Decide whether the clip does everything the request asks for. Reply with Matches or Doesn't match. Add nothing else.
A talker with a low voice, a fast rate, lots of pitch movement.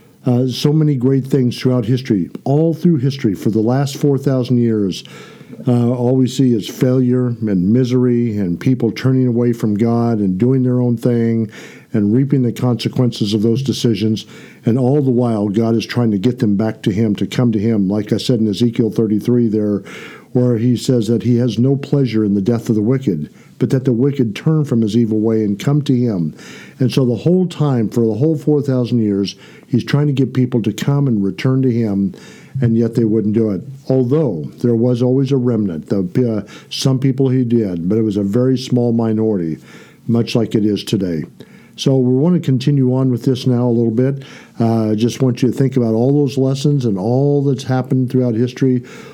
Doesn't match